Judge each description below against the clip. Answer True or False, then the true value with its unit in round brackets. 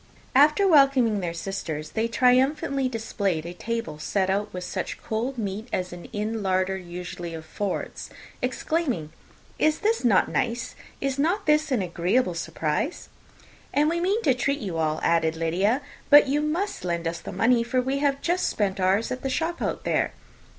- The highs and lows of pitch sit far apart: True (7.4 semitones)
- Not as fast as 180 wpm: True (170 wpm)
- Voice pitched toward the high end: True (225 Hz)